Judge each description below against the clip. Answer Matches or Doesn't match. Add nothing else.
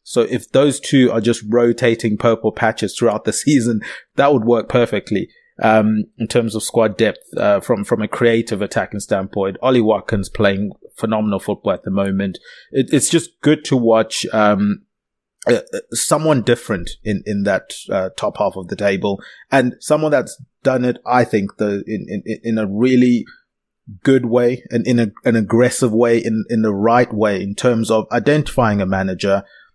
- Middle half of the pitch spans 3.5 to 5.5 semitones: Doesn't match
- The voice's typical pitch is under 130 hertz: Matches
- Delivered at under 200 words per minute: Matches